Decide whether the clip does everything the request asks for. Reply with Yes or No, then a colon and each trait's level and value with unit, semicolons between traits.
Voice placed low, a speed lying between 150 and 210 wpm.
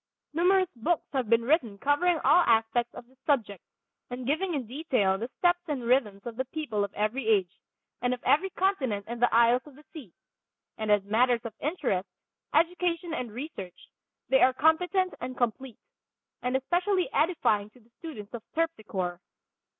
No: very high, 250 Hz; average, 170 wpm